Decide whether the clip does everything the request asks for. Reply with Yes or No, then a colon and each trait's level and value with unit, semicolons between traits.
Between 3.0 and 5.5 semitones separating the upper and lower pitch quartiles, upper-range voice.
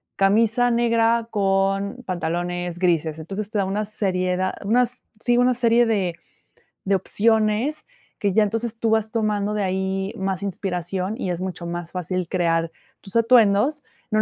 Yes: average, 3.6 semitones; high, 200 Hz